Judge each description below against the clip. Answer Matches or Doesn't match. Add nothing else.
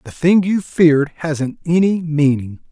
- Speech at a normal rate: Matches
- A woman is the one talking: Doesn't match